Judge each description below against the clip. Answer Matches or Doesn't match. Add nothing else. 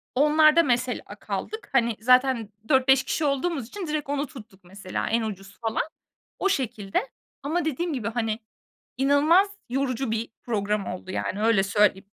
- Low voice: Doesn't match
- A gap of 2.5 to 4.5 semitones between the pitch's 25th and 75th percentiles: Doesn't match